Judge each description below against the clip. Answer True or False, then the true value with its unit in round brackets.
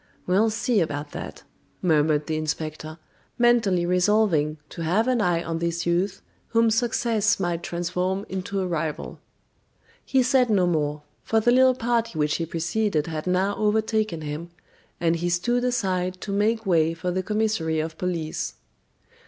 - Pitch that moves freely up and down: False (5.0 semitones)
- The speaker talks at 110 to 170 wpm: True (155 wpm)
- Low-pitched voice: False (180 Hz)